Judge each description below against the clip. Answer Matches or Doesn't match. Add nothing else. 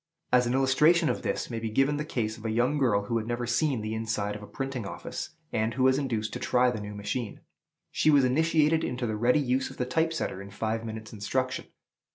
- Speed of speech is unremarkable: Doesn't match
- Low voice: Matches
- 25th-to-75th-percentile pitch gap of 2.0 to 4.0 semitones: Matches